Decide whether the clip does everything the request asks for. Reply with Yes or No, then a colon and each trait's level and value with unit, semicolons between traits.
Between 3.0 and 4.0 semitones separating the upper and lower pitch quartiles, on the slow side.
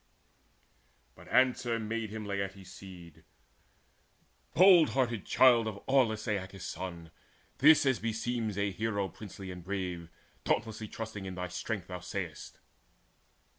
Yes: average, 3.6 semitones; slow, 130 wpm